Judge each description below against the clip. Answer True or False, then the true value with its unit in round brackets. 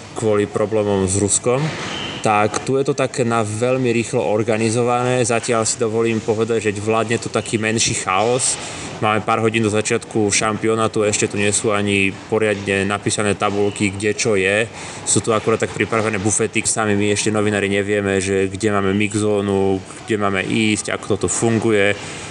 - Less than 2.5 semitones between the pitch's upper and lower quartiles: True (1.8 semitones)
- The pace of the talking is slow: False (165 wpm)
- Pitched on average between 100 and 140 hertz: True (110 Hz)